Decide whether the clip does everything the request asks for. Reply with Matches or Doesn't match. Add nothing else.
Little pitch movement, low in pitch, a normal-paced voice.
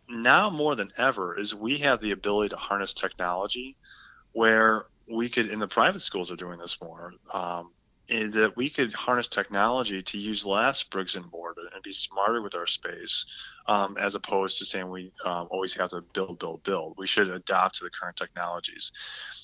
Doesn't match